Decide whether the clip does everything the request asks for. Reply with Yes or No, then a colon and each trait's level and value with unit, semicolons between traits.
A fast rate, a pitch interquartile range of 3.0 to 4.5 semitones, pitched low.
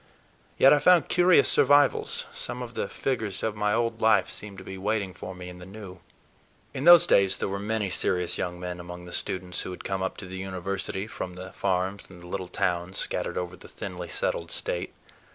Yes: fast, 210 wpm; average, 3.4 semitones; very low, 95 Hz